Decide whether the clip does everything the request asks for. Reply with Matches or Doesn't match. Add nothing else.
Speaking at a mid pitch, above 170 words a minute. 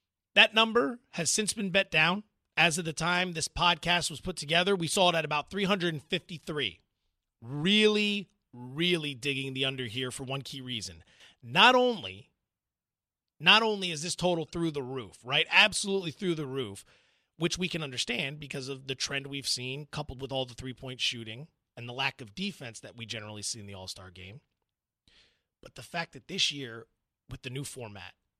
Matches